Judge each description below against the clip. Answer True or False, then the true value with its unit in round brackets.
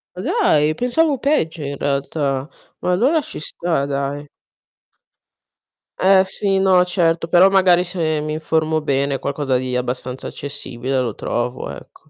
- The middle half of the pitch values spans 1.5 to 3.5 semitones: False (4.7 semitones)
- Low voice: False (155 Hz)